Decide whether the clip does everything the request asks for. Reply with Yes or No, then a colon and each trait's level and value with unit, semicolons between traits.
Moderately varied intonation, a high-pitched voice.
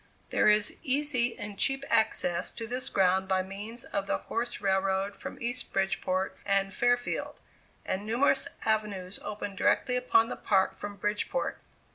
Yes: average, 3.7 semitones; high, 210 Hz